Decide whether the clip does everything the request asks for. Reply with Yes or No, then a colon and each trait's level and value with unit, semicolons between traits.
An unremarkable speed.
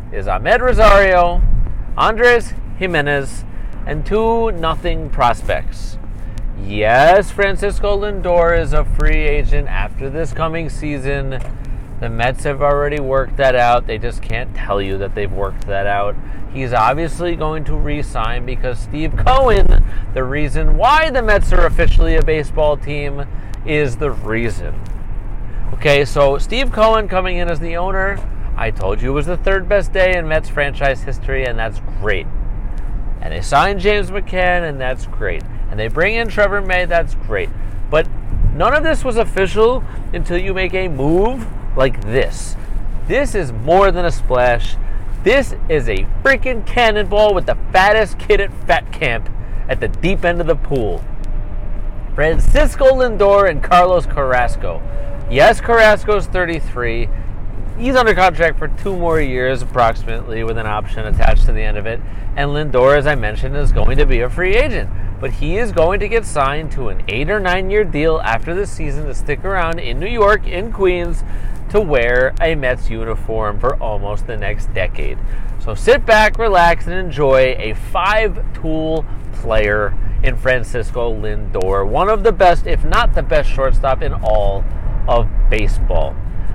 Yes: average, 165 wpm